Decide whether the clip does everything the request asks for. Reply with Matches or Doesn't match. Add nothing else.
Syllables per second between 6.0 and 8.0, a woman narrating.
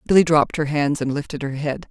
Matches